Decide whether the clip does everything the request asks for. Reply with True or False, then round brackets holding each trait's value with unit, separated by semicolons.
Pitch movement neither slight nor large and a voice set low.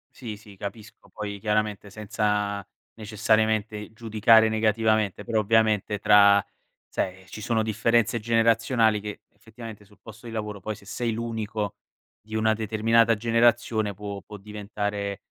False (1.5 semitones; 110 Hz)